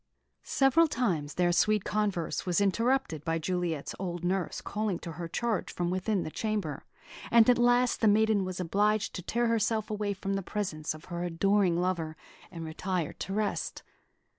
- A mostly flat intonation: No, average, 3.8 semitones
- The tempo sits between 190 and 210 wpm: No, average, 170 wpm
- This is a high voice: Yes, high, 195 Hz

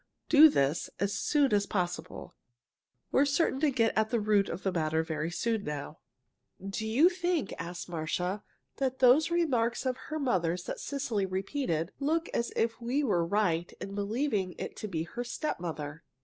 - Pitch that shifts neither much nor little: No, wide, 7.4 semitones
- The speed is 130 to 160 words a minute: No, average, 170 wpm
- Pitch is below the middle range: No, high, 215 Hz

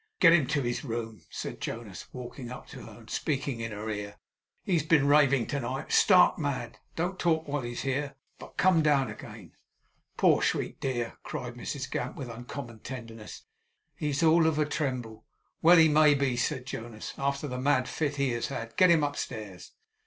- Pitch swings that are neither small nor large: Yes, average, 4.0 semitones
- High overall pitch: No, low, 135 Hz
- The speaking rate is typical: Yes, average, 190 wpm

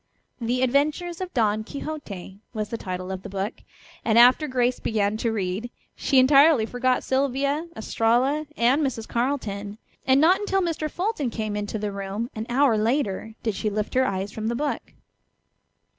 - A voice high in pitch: Yes, high, 240 Hz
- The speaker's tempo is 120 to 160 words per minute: No, average, 170 wpm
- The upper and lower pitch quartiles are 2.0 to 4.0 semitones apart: No, average, 4.8 semitones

